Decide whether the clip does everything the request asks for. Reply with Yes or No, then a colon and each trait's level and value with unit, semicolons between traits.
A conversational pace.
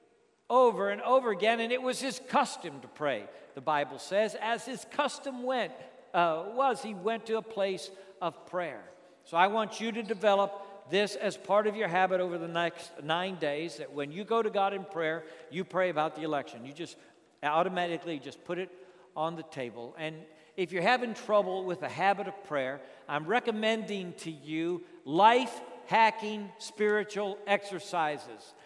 Yes: average, 175 wpm